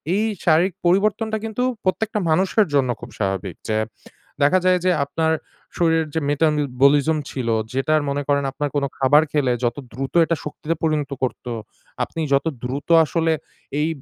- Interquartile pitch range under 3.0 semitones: No, average, 3.9 semitones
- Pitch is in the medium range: Yes, medium, 155 Hz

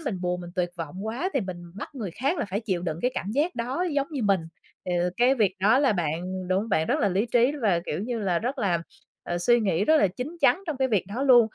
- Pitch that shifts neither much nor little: No, wide, 6.1 semitones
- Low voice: No, high, 210 Hz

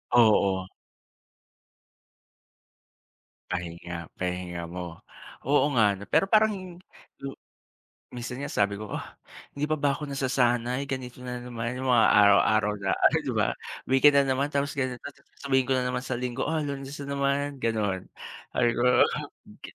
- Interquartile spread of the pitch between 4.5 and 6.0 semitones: Yes, average, 5.0 semitones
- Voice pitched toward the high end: No, low, 125 Hz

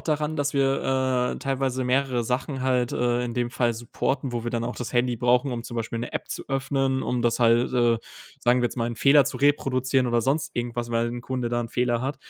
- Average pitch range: No, narrow, 1.9 semitones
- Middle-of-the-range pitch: No, low, 125 Hz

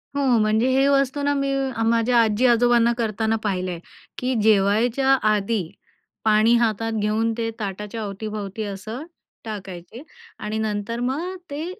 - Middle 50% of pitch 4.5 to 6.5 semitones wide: No, average, 2.7 semitones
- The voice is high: Yes, high, 225 Hz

